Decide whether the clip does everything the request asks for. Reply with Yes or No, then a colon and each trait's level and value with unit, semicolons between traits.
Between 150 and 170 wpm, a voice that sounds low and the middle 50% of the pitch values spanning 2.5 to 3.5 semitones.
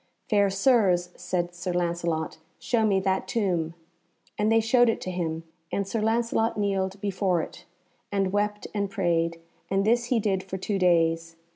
No: average, 165 wpm; high, 190 Hz; average, 3.1 semitones